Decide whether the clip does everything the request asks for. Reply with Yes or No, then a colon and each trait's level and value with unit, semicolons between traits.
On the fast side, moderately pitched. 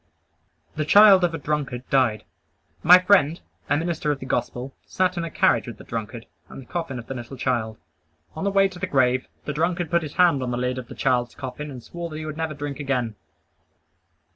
Yes: fast, 220 wpm; medium, 145 Hz